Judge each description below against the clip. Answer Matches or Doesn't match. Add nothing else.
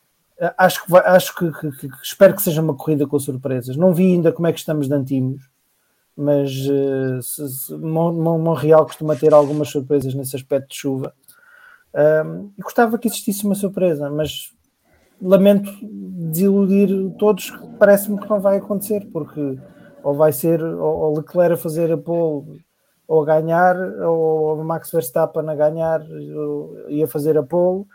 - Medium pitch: Matches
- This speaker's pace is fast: Doesn't match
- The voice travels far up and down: Doesn't match